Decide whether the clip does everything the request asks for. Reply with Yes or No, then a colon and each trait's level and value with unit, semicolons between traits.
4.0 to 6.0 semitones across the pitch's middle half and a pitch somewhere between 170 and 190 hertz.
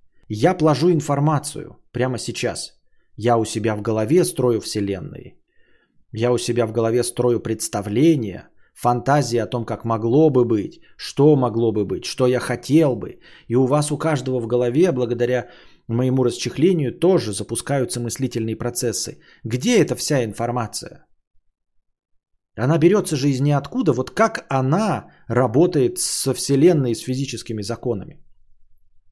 No: average, 4.3 semitones; low, 125 Hz